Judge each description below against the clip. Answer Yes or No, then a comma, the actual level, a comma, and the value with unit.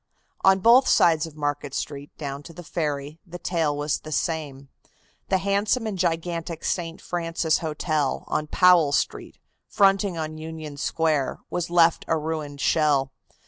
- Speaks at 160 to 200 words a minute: No, average, 150 wpm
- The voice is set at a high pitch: No, medium, 160 Hz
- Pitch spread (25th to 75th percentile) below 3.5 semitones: Yes, average, 3.0 semitones